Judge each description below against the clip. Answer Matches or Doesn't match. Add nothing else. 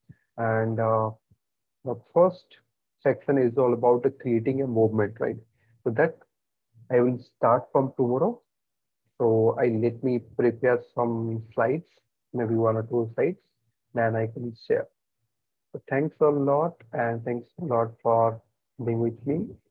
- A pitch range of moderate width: Doesn't match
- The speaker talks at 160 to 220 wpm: Doesn't match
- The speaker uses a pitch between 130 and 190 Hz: Doesn't match